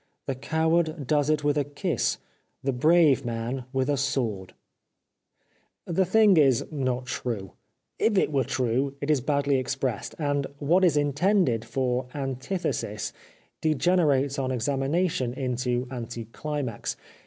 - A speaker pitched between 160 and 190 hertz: No, low, 135 Hz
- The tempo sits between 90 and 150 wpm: Yes, average, 140 wpm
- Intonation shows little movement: No, average, 3.4 semitones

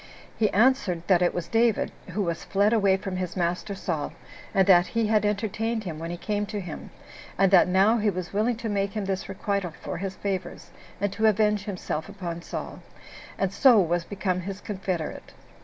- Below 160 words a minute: No, average, 195 wpm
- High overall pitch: Yes, high, 195 Hz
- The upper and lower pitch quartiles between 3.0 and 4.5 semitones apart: No, narrow, 2.6 semitones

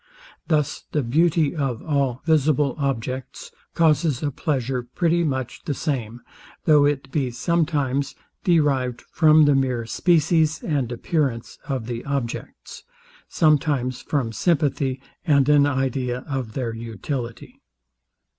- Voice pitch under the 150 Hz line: Yes, medium, 140 Hz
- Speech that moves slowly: Yes, slow, 120 wpm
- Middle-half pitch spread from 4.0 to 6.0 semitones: No, average, 3.3 semitones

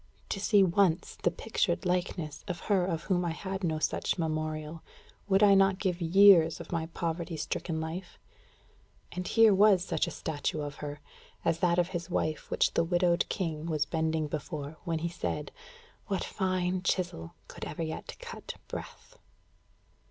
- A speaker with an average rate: Yes, average, 165 wpm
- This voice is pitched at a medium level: Yes, medium, 170 Hz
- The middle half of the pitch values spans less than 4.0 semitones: Yes, average, 2.9 semitones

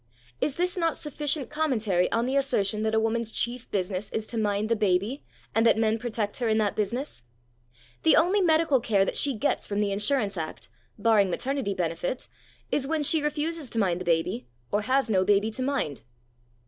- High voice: Yes, high, 225 Hz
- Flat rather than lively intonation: No, wide, 5.4 semitones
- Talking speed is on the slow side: No, average, 195 wpm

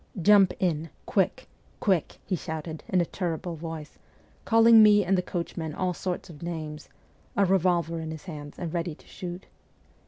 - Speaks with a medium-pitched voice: Yes, medium, 175 Hz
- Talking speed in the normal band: Yes, average, 180 wpm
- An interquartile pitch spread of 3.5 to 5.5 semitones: No, average, 2.7 semitones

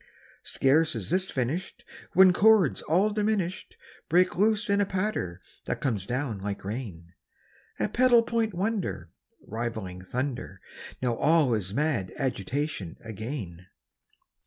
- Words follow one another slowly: Yes, slow, 125 wpm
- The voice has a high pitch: No, medium, 145 Hz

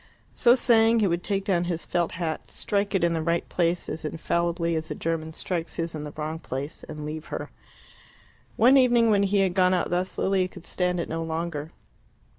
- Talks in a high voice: No, medium, 170 Hz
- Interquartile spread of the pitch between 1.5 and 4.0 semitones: Yes, average, 3.1 semitones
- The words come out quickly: Yes, fast, 210 wpm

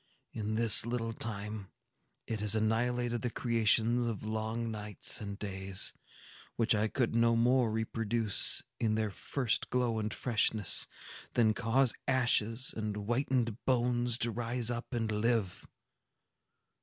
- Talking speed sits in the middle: No, slow, 130 wpm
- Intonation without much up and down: Yes, narrow, 2.0 semitones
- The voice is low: Yes, low, 115 Hz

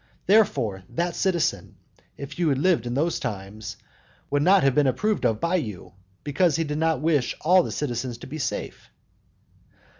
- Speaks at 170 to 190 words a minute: Yes, average, 175 wpm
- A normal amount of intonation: No, wide, 5.8 semitones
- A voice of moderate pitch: Yes, medium, 150 Hz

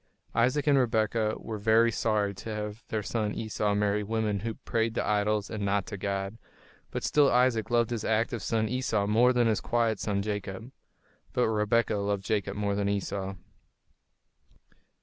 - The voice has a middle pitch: No, low, 110 Hz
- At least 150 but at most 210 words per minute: Yes, average, 170 wpm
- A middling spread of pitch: No, narrow, 2.1 semitones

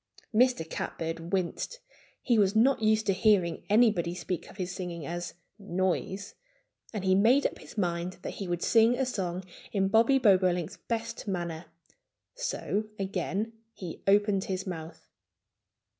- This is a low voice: No, high, 190 Hz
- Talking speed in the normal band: Yes, average, 145 wpm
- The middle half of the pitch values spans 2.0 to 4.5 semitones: Yes, average, 3.9 semitones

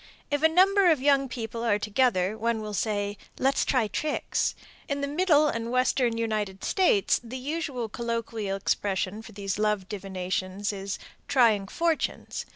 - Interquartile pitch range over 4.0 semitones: Yes, average, 5.2 semitones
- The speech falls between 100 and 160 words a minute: Yes, average, 155 wpm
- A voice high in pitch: Yes, high, 230 Hz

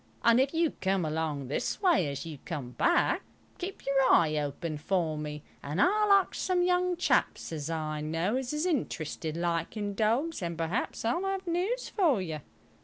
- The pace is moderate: Yes, average, 180 wpm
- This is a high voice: Yes, high, 195 Hz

